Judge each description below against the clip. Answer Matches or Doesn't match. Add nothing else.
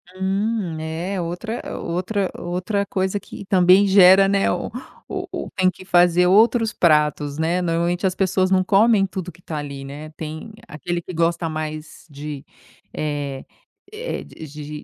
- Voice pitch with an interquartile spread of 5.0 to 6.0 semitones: Doesn't match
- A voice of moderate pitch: Matches